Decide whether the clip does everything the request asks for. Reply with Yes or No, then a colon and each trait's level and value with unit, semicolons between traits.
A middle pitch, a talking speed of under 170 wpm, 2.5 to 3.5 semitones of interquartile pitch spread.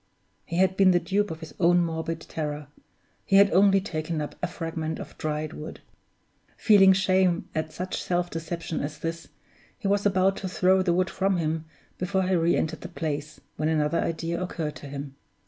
No: medium, 170 Hz; average, 190 wpm; average, 3.0 semitones